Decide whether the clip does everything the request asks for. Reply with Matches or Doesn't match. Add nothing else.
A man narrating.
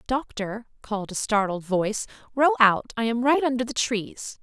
Doesn't match